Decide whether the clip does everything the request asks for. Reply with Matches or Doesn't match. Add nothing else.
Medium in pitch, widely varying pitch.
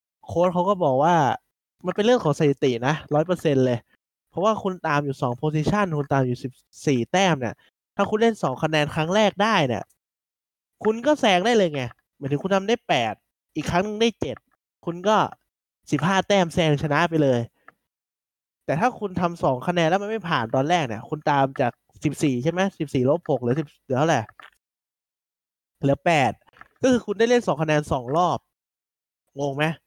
Matches